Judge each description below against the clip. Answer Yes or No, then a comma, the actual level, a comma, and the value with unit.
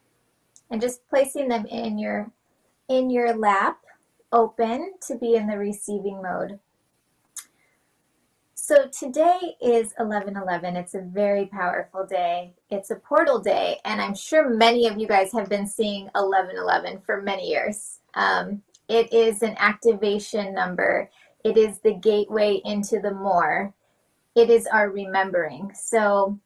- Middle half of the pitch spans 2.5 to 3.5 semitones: Yes, average, 2.8 semitones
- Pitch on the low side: No, high, 210 Hz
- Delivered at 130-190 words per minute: Yes, average, 145 wpm